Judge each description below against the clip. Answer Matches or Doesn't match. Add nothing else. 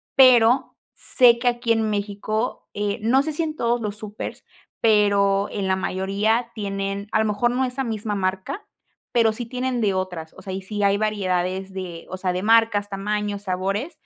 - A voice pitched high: Matches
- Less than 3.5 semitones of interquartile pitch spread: Matches